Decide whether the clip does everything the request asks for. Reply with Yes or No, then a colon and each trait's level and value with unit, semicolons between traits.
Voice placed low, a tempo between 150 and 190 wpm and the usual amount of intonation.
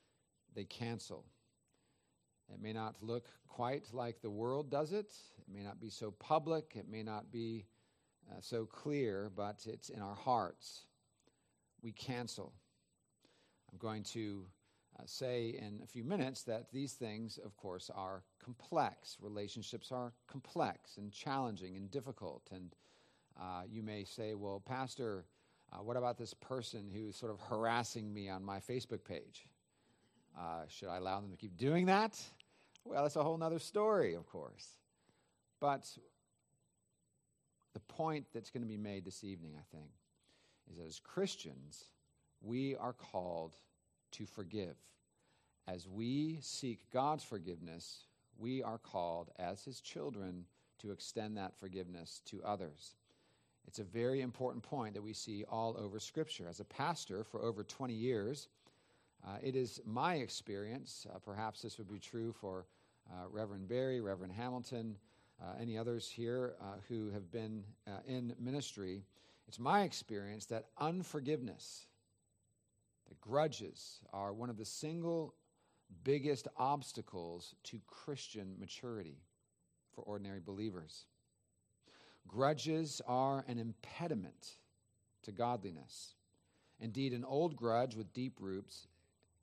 No: low, 110 Hz; average, 140 wpm; average, 4.2 semitones